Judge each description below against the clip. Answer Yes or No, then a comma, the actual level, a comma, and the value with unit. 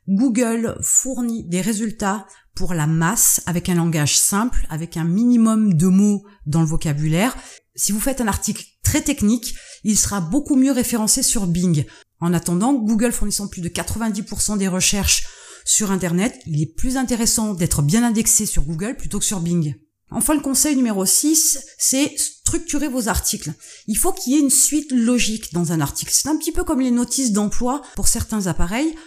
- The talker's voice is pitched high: Yes, high, 215 Hz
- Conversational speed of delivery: Yes, average, 180 wpm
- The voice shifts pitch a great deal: Yes, wide, 6.3 semitones